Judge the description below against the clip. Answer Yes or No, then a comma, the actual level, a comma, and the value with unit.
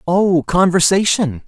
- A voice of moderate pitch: Yes, medium, 175 Hz